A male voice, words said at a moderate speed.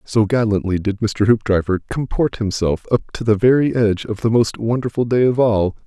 Yes: male; average, 195 wpm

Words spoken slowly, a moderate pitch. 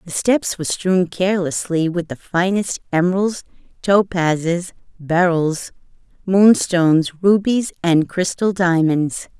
Yes: slow, 100 wpm; medium, 175 Hz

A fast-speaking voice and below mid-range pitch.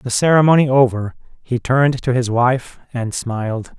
No: average, 160 wpm; low, 125 Hz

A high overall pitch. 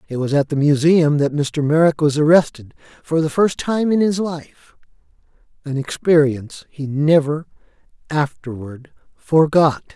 No: medium, 150 Hz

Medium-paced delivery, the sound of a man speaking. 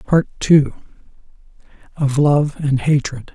No: slow, 110 wpm; male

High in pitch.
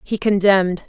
Yes: high, 195 Hz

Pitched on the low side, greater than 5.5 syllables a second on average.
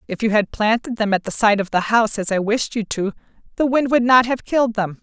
No: high, 220 Hz; 5.9 syllables/s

